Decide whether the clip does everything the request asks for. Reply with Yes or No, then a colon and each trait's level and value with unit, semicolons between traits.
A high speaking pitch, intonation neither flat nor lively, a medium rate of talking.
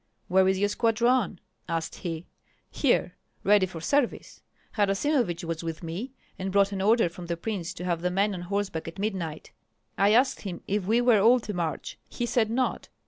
Yes: high, 195 Hz; average, 4.3 semitones; average, 190 wpm